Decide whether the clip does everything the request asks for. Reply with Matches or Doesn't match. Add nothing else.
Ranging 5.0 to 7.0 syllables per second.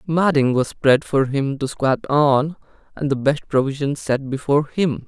Doesn't match